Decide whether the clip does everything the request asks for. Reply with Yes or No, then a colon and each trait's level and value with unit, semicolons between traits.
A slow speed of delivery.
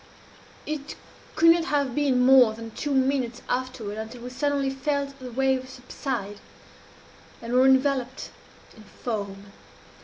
Yes: slow, 130 wpm